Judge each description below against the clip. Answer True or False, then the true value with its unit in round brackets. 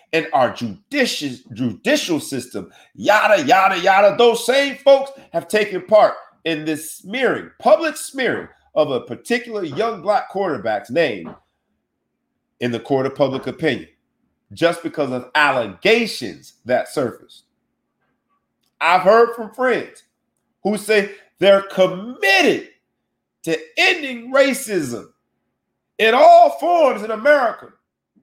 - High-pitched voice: True (215 Hz)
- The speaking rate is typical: False (115 wpm)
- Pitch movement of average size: False (8.3 semitones)